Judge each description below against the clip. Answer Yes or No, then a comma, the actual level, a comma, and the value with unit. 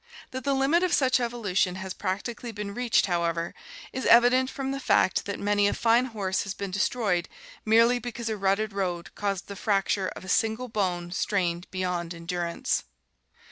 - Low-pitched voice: No, high, 205 Hz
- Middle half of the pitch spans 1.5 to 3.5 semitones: No, average, 4.4 semitones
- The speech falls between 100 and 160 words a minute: No, average, 175 wpm